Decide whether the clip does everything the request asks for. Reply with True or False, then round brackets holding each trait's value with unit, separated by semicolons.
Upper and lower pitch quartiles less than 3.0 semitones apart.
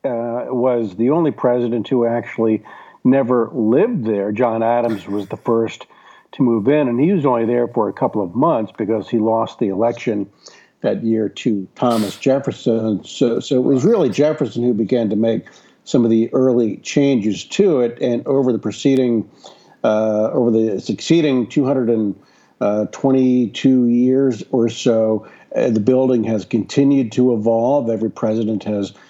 True (2.4 semitones)